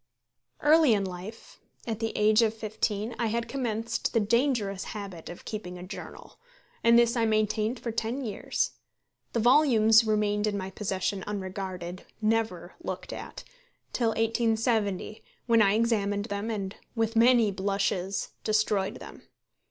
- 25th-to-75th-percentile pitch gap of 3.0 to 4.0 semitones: No, narrow, 2.4 semitones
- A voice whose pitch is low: No, high, 215 Hz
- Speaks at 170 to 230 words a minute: No, average, 145 wpm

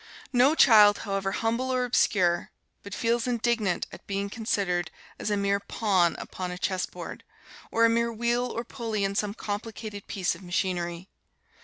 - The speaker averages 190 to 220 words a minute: No, average, 165 wpm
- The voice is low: No, high, 205 Hz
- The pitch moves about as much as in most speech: Yes, average, 3.4 semitones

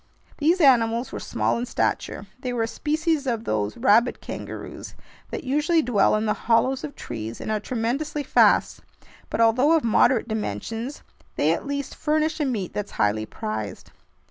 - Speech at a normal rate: Yes, average, 170 wpm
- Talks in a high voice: Yes, high, 240 Hz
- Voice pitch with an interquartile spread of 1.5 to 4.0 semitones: No, wide, 5.4 semitones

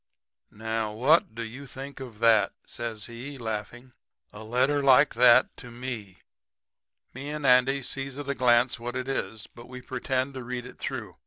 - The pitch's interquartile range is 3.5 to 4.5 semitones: No, average, 2.7 semitones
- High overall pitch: No, low, 125 Hz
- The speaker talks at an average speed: Yes, average, 175 wpm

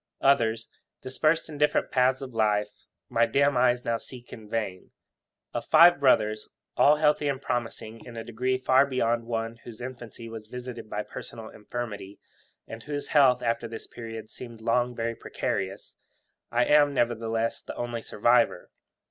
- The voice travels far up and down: No, narrow, 2.4 semitones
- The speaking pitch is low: Yes, low, 120 Hz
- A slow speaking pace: No, average, 155 wpm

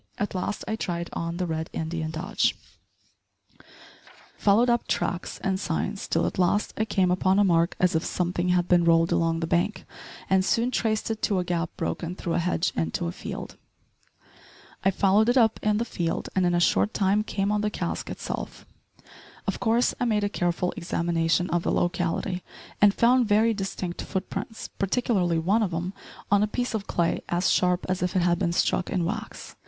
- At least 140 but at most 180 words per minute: No, average, 195 wpm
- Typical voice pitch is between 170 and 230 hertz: Yes, medium, 185 Hz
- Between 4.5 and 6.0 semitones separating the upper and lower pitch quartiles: No, average, 3.4 semitones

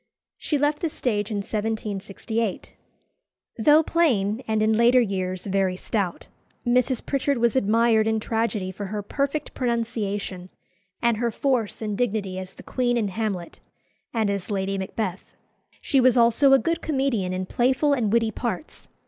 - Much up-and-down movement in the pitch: No, average, 3.9 semitones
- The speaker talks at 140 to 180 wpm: Yes, average, 155 wpm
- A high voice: Yes, high, 225 Hz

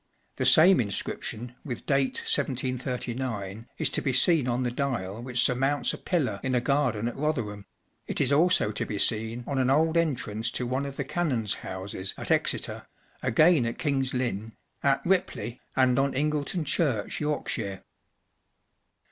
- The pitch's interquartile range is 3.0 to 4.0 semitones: Yes, average, 3.7 semitones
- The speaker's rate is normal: Yes, average, 165 wpm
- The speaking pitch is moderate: No, low, 130 Hz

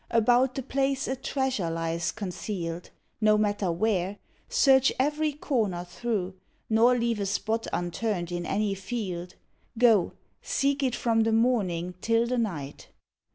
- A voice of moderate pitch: No, high, 220 Hz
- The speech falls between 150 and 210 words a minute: No, average, 140 wpm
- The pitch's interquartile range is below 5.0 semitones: No, wide, 5.5 semitones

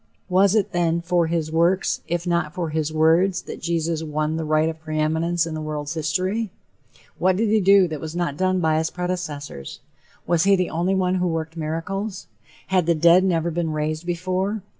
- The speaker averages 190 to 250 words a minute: Yes, average, 195 wpm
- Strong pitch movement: No, narrow, 2.5 semitones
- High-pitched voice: No, medium, 170 Hz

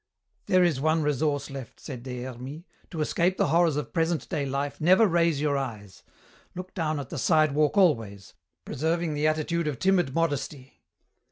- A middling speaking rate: Yes, average, 170 wpm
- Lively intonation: No, average, 3.6 semitones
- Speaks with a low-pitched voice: No, medium, 150 Hz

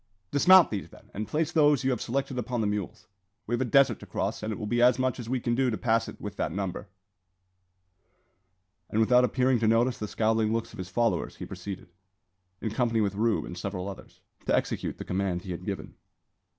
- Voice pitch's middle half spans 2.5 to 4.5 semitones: Yes, average, 3.5 semitones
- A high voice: No, low, 115 Hz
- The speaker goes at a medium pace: No, fast, 220 wpm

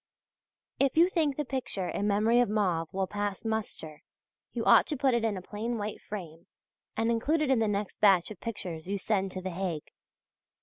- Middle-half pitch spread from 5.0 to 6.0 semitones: No, average, 3.9 semitones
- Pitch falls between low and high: No, high, 210 Hz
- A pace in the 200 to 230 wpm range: Yes, fast, 205 wpm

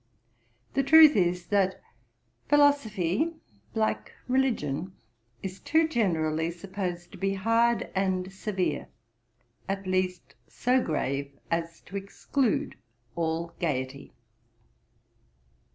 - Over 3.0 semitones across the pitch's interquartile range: Yes, average, 5.1 semitones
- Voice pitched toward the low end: No, high, 190 Hz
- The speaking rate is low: Yes, slow, 95 wpm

